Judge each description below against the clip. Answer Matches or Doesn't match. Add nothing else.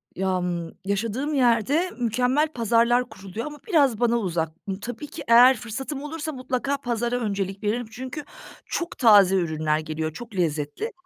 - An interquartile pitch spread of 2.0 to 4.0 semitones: Doesn't match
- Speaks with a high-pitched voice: Matches